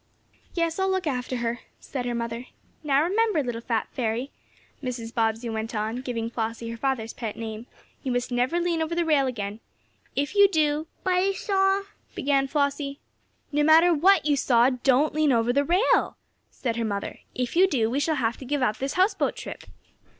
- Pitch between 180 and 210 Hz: No, very high, 270 Hz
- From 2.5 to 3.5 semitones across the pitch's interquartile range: No, average, 5.3 semitones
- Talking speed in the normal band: Yes, average, 195 wpm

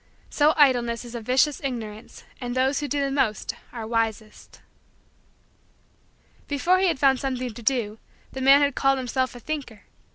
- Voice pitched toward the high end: Yes, very high, 255 Hz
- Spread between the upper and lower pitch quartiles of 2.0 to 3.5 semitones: Yes, average, 3.2 semitones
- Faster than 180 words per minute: No, average, 165 wpm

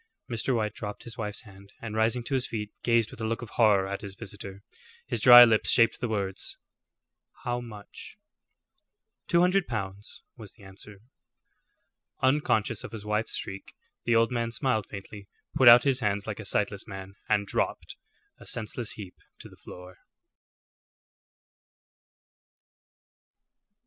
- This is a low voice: Yes, low, 110 Hz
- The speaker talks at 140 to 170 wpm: Yes, average, 150 wpm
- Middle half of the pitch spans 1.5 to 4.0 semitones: Yes, average, 2.8 semitones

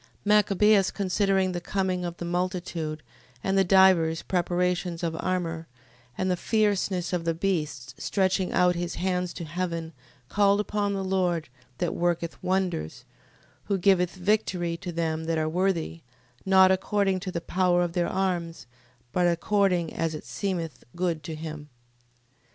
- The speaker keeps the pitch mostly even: Yes, narrow, 2.3 semitones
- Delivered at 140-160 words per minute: Yes, average, 150 wpm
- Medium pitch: Yes, medium, 180 Hz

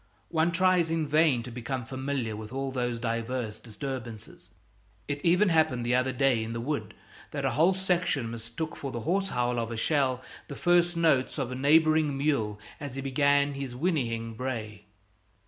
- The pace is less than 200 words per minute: Yes, average, 180 wpm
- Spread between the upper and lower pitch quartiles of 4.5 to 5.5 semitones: Yes, average, 4.8 semitones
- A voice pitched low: Yes, low, 130 Hz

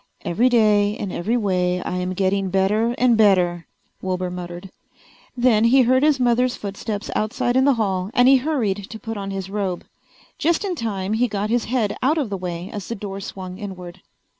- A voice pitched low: No, high, 205 Hz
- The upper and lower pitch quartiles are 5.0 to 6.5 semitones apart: No, average, 4.3 semitones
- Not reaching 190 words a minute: No, average, 195 wpm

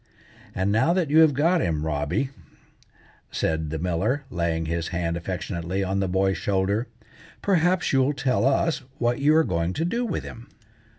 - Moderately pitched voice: No, low, 100 Hz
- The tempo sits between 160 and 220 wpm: Yes, average, 170 wpm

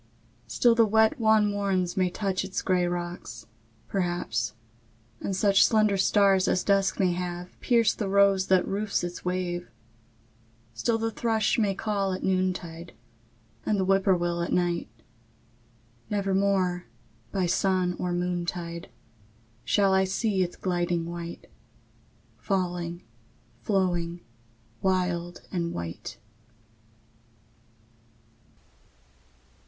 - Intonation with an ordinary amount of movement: No, narrow, 2.2 semitones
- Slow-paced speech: Yes, slow, 110 wpm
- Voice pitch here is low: No, medium, 185 Hz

